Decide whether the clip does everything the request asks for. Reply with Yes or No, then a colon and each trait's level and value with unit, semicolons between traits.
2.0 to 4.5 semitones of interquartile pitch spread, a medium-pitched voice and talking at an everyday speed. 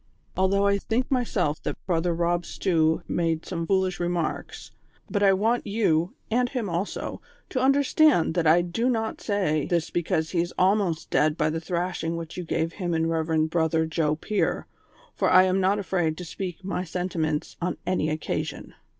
Yes: average, 3.3 semitones; medium, 175 Hz; average, 180 wpm